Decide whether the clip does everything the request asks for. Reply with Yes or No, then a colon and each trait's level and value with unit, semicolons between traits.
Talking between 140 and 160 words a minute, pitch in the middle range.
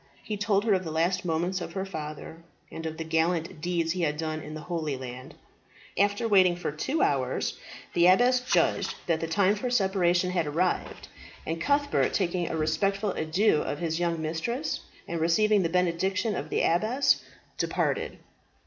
No: average, 175 wpm; medium, 175 Hz